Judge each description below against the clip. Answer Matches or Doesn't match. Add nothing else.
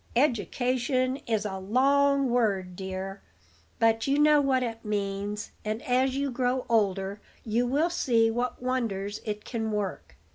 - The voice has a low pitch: Doesn't match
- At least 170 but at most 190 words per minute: Doesn't match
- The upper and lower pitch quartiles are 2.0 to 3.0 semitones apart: Doesn't match